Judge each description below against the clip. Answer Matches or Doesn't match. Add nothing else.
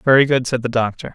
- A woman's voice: Doesn't match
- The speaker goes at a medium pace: Doesn't match